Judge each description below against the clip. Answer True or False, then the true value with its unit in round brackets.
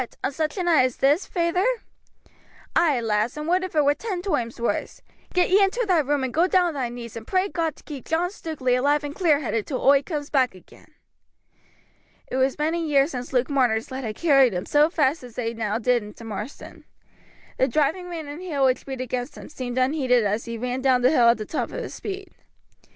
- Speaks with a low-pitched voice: False (275 Hz)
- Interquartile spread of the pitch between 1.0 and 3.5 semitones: False (4.8 semitones)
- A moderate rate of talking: False (225 wpm)